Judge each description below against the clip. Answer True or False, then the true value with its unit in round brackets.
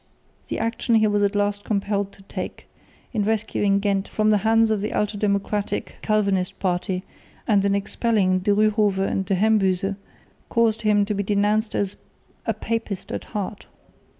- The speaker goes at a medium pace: True (165 wpm)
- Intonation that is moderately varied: False (1.5 semitones)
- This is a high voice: True (205 Hz)